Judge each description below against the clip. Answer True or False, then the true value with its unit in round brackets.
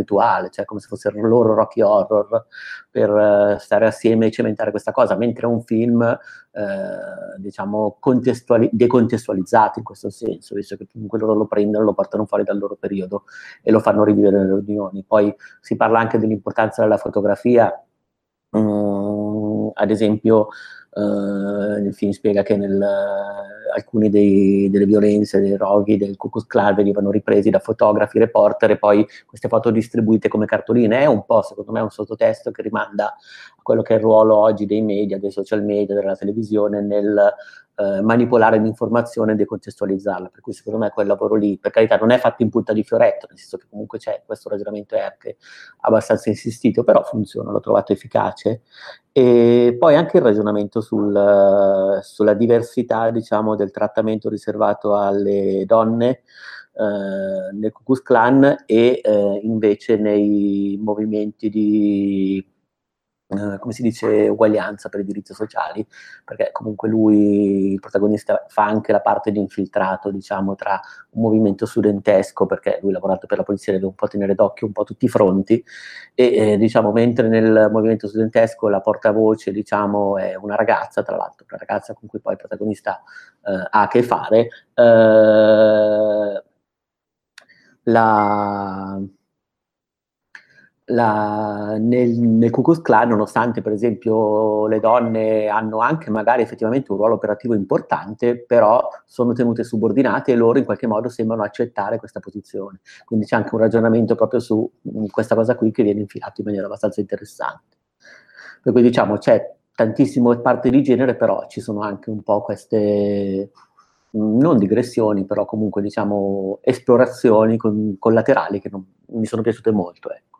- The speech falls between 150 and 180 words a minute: True (160 wpm)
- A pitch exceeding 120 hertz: False (105 Hz)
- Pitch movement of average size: False (1.9 semitones)